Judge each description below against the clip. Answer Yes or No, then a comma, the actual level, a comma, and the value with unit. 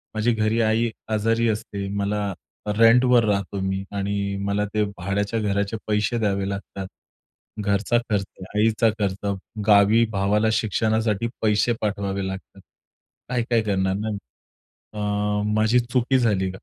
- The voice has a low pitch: Yes, low, 105 Hz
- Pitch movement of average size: No, narrow, 2.3 semitones